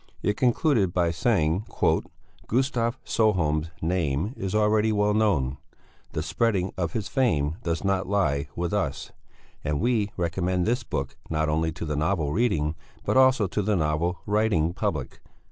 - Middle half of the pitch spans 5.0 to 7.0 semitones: Yes, wide, 5.4 semitones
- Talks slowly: No, average, 150 wpm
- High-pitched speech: No, very low, 95 Hz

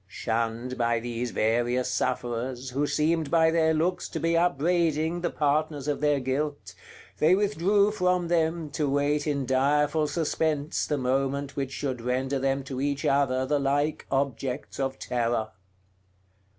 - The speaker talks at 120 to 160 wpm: Yes, average, 150 wpm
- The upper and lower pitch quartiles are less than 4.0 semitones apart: Yes, average, 3.6 semitones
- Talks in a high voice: No, medium, 140 Hz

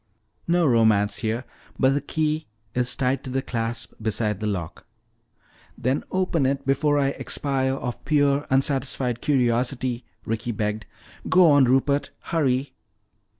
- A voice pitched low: Yes, low, 130 Hz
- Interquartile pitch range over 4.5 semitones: No, average, 3.3 semitones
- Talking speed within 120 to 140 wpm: Yes, slow, 135 wpm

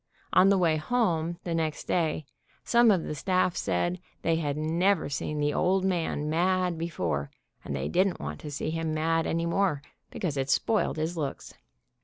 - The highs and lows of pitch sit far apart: No, average, 3.2 semitones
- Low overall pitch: No, medium, 165 Hz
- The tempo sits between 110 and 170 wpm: No, average, 180 wpm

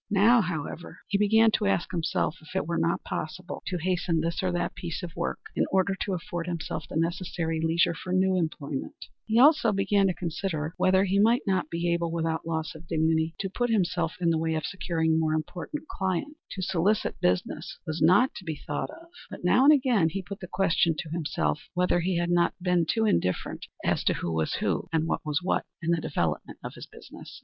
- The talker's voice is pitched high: No, medium, 175 Hz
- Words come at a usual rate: No, fast, 215 wpm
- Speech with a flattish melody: No, average, 3.0 semitones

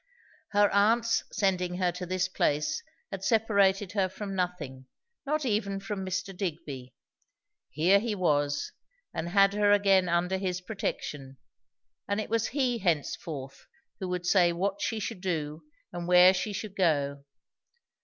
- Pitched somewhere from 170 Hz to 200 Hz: Yes, medium, 185 Hz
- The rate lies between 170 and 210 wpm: No, average, 145 wpm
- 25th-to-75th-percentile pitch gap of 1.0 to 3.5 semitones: Yes, average, 2.8 semitones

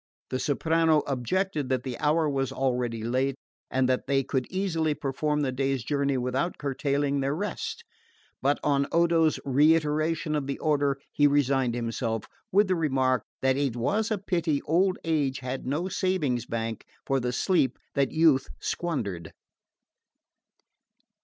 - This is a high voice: No, medium, 140 Hz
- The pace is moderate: Yes, average, 145 wpm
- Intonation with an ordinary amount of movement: Yes, average, 3.5 semitones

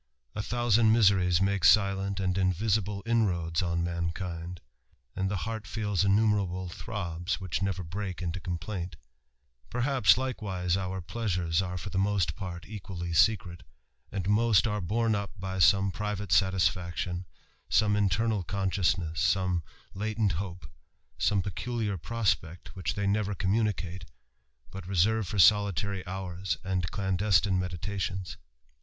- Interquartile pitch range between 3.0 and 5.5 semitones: No, narrow, 2.6 semitones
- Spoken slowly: Yes, slow, 130 wpm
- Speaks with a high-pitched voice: No, very low, 95 Hz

